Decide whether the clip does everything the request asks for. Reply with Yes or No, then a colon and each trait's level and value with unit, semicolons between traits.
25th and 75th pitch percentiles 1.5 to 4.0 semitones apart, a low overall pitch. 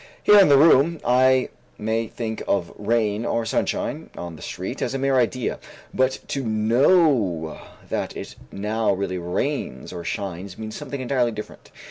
No: average, 4.7 semitones; low, 115 Hz